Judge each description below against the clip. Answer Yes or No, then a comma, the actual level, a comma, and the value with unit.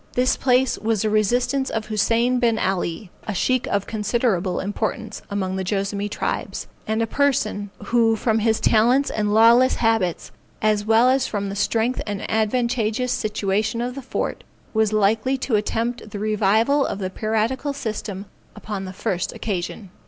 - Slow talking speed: No, average, 160 wpm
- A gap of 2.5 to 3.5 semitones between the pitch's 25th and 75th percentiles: Yes, average, 2.8 semitones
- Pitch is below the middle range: No, high, 220 Hz